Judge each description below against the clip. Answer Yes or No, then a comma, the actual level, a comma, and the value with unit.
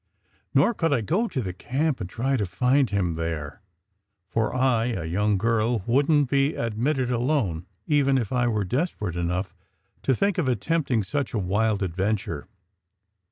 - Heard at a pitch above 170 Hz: No, low, 115 Hz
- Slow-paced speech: No, average, 165 wpm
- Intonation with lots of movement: Yes, wide, 6.0 semitones